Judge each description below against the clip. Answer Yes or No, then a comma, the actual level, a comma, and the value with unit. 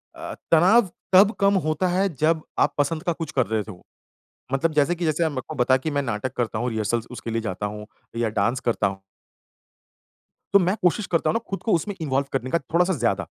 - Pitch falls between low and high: Yes, medium, 145 Hz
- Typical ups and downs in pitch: No, wide, 6.7 semitones